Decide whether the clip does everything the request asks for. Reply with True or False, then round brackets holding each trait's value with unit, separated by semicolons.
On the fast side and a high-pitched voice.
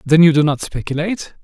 False (210 wpm; 155 Hz)